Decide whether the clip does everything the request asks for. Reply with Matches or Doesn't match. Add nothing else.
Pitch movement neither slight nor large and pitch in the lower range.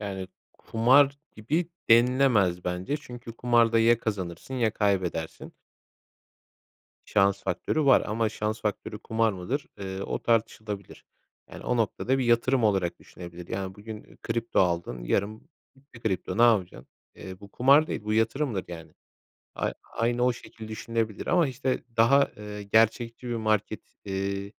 Matches